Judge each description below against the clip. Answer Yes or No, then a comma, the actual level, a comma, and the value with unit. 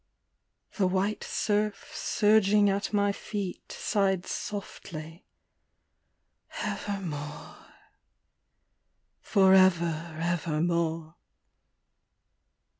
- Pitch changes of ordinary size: Yes, average, 3.4 semitones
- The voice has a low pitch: No, high, 190 Hz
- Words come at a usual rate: No, slow, 65 wpm